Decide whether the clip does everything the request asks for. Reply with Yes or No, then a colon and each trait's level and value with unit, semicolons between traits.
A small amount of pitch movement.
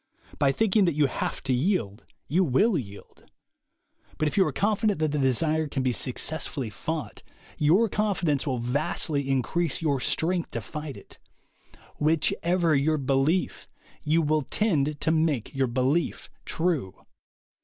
No: average, 4.0 semitones